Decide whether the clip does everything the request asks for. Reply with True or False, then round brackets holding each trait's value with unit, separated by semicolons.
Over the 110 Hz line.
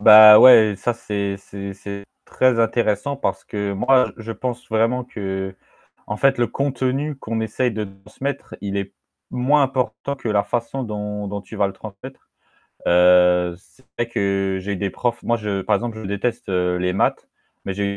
False (105 Hz)